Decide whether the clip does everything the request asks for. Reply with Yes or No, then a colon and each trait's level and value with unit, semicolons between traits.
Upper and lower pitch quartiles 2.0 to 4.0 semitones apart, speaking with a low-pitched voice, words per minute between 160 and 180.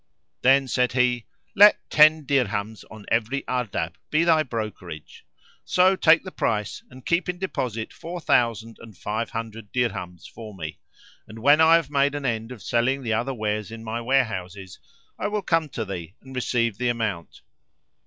No: average, 4.4 semitones; low, 120 Hz; average, 175 wpm